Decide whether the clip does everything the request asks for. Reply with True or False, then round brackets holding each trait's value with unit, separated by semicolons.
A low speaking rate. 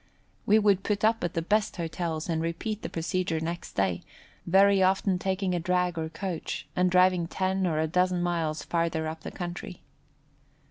False (180 wpm)